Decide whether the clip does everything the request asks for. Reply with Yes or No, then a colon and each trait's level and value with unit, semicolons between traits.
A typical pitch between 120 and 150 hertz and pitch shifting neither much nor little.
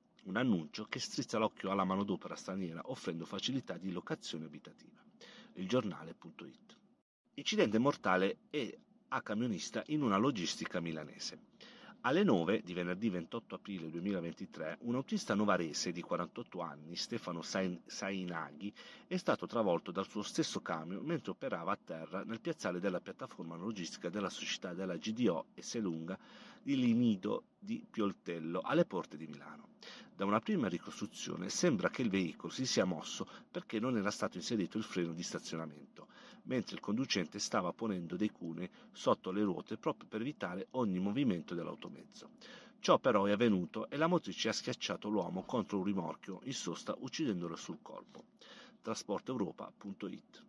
No: very low, 95 Hz; average, 4.7 semitones